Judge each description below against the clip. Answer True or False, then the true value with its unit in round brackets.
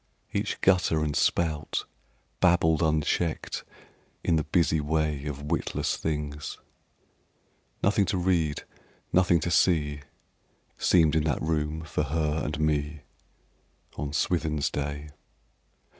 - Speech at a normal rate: False (115 wpm)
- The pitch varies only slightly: True (2.0 semitones)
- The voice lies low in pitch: True (75 Hz)